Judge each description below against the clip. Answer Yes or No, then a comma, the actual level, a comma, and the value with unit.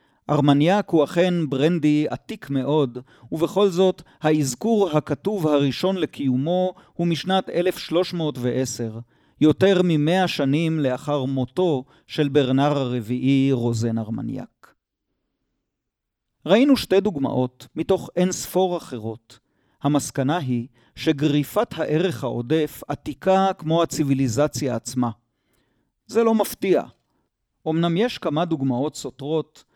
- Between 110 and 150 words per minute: No, slow, 100 wpm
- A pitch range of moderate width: Yes, average, 5.0 semitones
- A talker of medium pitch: Yes, medium, 150 Hz